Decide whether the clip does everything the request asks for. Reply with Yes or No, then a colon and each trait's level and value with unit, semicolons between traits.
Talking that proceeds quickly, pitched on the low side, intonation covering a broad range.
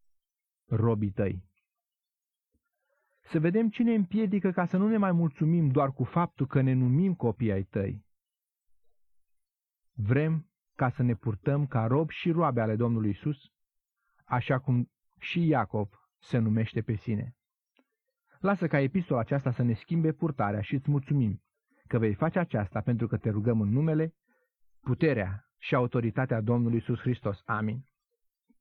No: average, 145 wpm; low, 130 Hz; wide, 6.6 semitones